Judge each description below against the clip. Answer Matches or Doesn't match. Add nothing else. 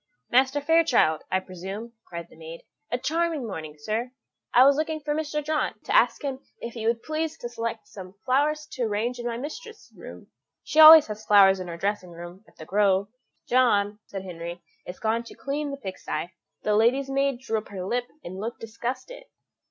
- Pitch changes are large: Matches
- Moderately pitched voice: Doesn't match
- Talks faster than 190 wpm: Matches